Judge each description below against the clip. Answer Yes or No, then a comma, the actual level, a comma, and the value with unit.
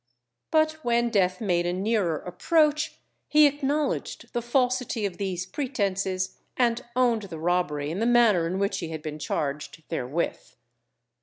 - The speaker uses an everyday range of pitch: No, wide, 6.1 semitones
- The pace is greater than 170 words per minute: No, average, 150 wpm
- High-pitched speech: Yes, high, 200 Hz